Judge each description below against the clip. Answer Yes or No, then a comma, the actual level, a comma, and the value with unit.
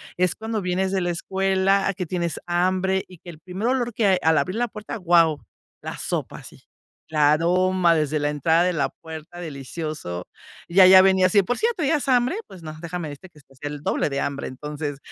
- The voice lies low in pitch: No, medium, 175 Hz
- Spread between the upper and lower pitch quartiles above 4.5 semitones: No, average, 3.6 semitones